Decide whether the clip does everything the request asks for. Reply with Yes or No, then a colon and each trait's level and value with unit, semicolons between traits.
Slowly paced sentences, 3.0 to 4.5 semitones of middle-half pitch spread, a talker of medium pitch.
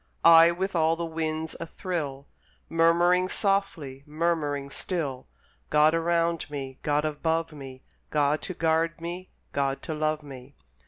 No: slow, 130 wpm; narrow, 2.6 semitones; medium, 160 Hz